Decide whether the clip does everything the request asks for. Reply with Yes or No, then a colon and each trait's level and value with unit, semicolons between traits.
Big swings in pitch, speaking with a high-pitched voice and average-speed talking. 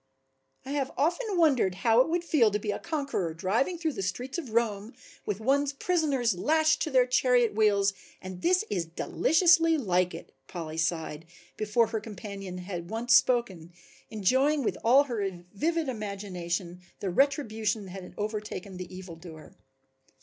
Yes: wide, 7.0 semitones; high, 220 Hz; average, 155 wpm